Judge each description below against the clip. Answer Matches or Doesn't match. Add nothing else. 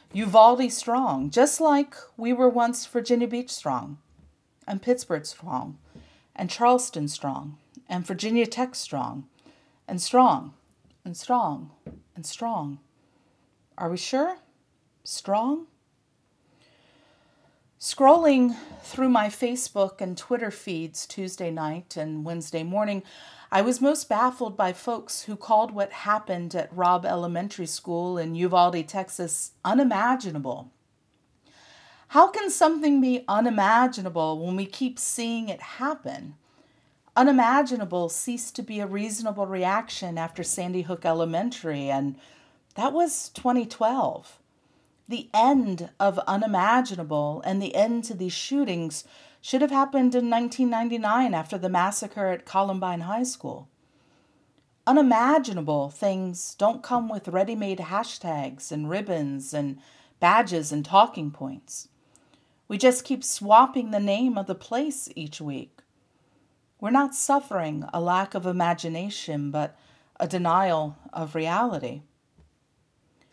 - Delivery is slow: Matches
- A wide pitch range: Matches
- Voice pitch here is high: Matches